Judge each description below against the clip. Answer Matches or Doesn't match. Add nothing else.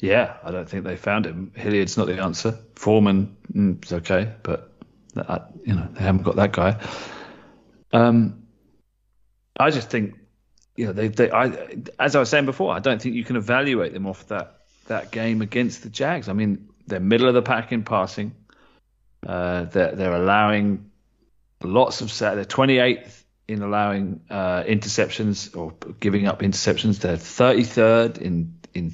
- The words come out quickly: Doesn't match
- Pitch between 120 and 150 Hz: Doesn't match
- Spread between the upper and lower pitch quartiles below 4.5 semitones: Matches